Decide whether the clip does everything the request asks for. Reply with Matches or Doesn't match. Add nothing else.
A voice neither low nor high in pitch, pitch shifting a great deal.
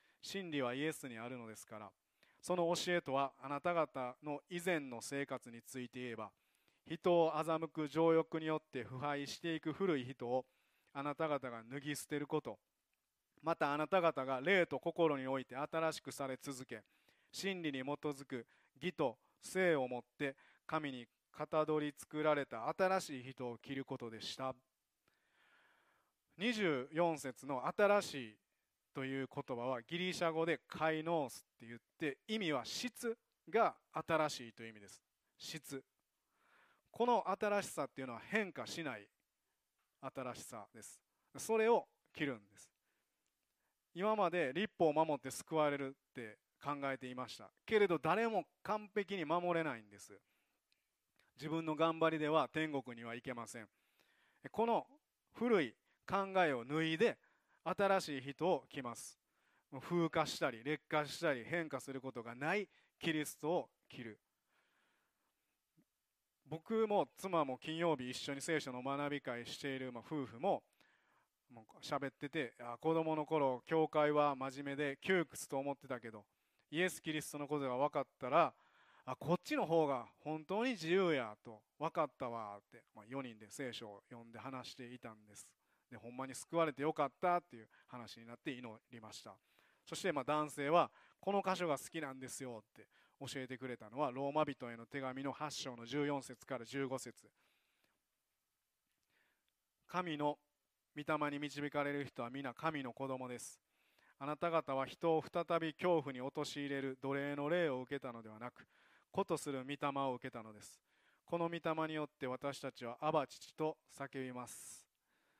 Doesn't match